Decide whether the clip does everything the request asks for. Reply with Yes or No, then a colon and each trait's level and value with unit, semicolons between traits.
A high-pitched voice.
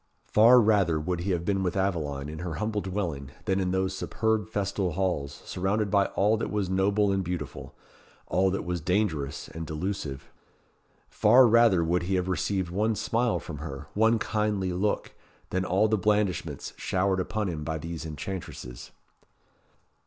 No: very low, 95 Hz